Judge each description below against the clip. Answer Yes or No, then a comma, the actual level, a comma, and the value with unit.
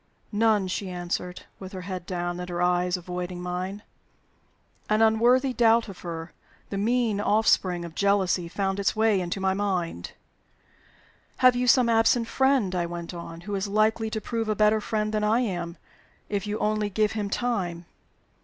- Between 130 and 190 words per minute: Yes, average, 175 wpm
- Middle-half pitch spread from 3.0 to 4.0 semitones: Yes, average, 3.6 semitones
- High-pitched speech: Yes, high, 200 Hz